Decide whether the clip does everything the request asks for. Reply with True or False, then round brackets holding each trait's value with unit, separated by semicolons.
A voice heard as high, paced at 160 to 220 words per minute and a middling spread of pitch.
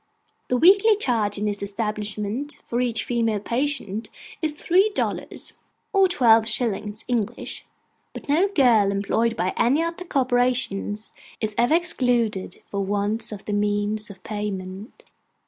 False (225 Hz; 140 wpm; 4.1 semitones)